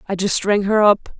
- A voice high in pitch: Yes, high, 200 Hz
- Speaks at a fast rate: Yes, fast, 250 wpm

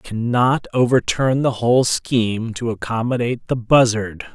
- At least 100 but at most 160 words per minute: Yes, average, 140 wpm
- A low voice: Yes, low, 120 Hz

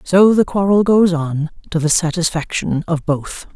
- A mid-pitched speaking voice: Yes, medium, 170 Hz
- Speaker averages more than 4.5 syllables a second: No, 4.4 syllables/s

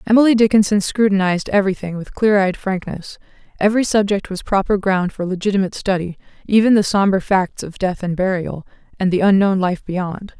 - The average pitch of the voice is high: Yes, high, 195 Hz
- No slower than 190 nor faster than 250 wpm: No, average, 165 wpm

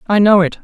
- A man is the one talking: No, female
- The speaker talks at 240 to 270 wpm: No, fast, 285 wpm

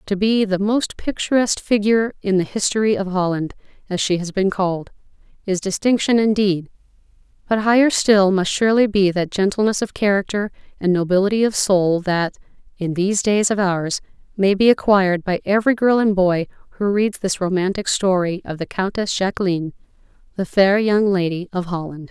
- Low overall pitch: No, high, 195 Hz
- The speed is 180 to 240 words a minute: No, average, 170 wpm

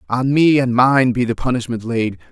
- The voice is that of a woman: No, male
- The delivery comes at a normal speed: No, fast, 210 wpm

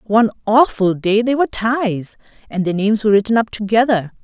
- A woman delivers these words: Yes, female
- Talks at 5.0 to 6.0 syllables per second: Yes, 5.8 syllables/s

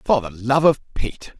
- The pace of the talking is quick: Yes, fast, 215 wpm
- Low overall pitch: Yes, low, 125 Hz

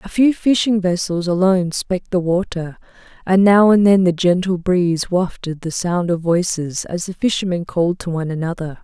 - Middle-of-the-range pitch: Yes, medium, 180 Hz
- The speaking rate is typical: Yes, average, 185 wpm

